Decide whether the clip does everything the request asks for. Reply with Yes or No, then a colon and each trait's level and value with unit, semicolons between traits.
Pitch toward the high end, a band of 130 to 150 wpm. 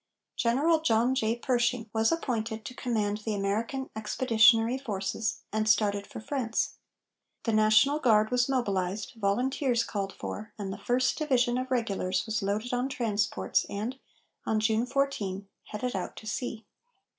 Yes: high, 225 Hz; average, 145 wpm